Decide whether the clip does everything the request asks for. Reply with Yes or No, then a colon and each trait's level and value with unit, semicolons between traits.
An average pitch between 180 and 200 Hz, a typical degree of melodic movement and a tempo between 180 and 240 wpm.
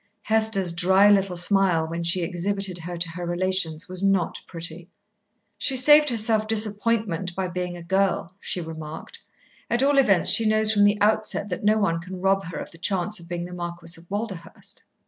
Yes: medium, 185 Hz; average, 3.4 semitones; average, 185 wpm